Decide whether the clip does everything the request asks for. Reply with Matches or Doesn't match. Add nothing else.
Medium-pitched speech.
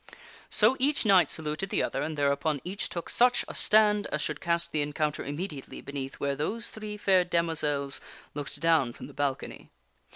Matches